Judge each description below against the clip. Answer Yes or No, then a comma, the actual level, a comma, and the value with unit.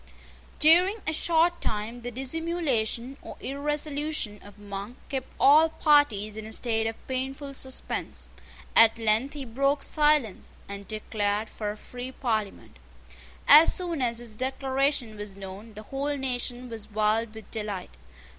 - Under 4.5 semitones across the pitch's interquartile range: No, average, 4.9 semitones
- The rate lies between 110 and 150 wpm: Yes, average, 145 wpm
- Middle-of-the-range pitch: No, high, 245 Hz